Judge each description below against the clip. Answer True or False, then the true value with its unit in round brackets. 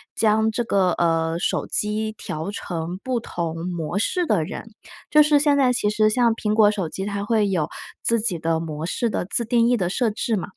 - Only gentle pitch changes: False (5.0 semitones)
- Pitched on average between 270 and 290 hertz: False (210 Hz)